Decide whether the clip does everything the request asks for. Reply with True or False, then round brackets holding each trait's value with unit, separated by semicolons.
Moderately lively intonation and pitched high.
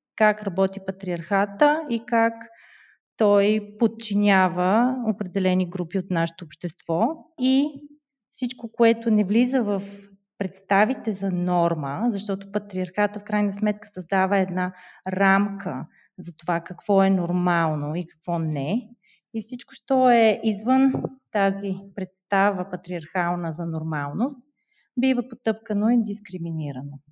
True (4.0 semitones; 200 Hz)